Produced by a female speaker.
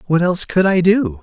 No: male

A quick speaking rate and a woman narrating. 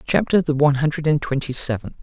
No: fast, 210 wpm; male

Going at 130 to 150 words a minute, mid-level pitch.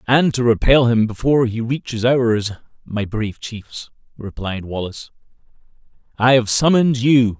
No: average, 140 wpm; low, 120 Hz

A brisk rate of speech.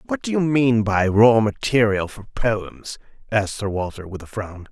No: average, 190 wpm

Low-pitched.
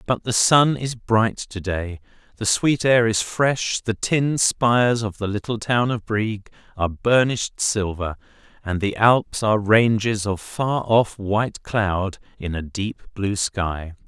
Yes: low, 105 Hz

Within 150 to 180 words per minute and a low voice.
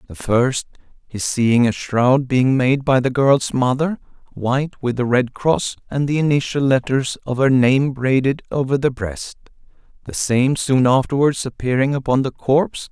Yes: average, 165 wpm; low, 130 Hz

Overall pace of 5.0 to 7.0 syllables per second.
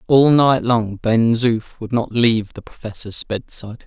No: 4.6 syllables/s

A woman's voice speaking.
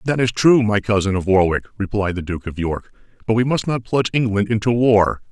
No: male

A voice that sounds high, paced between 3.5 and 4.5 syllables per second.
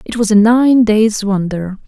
Yes: high, 215 Hz; 4.1 syllables/s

